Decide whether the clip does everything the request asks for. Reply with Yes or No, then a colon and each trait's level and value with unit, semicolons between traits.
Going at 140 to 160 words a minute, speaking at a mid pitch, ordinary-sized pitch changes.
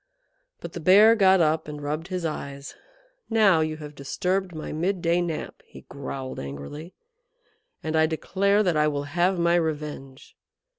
Yes: average, 155 wpm; medium, 160 Hz; average, 3.6 semitones